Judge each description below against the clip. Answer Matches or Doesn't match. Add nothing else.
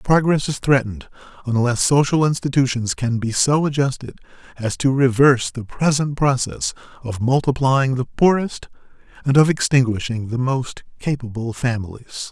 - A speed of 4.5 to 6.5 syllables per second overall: Matches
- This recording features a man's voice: Matches